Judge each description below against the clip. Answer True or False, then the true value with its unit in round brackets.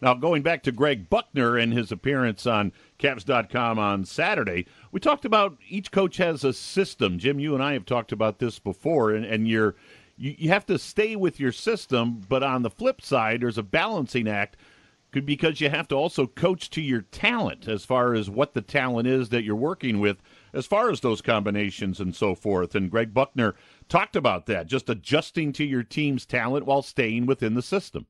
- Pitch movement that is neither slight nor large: True (4.8 semitones)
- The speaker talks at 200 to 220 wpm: True (205 wpm)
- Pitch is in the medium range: False (125 Hz)